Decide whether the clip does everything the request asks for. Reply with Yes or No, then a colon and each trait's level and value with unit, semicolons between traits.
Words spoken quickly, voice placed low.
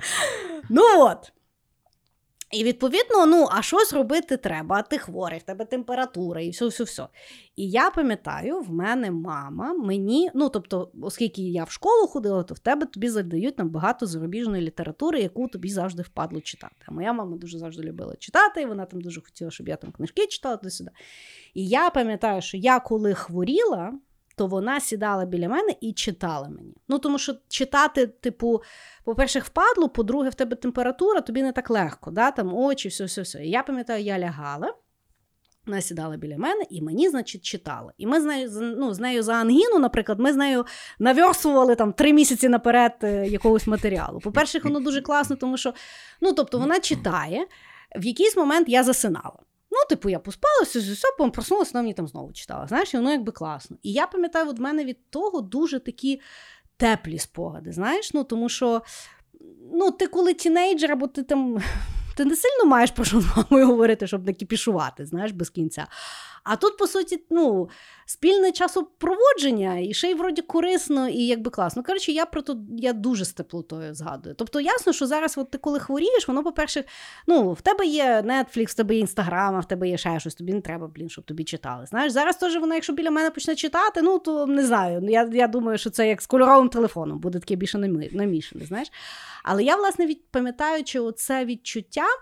No: fast, 190 wpm; high, 245 Hz